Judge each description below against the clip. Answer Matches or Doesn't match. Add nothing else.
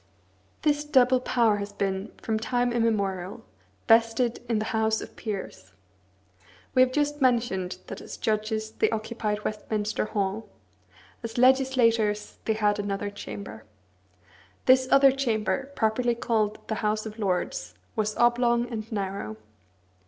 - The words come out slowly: Matches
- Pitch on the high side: Matches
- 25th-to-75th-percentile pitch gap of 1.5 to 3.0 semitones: Matches